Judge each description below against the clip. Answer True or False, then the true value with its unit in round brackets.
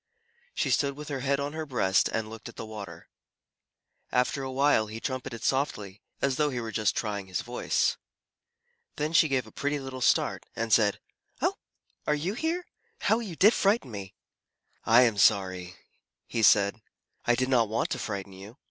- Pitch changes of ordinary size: True (5.0 semitones)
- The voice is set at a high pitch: False (120 Hz)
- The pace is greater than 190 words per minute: False (185 wpm)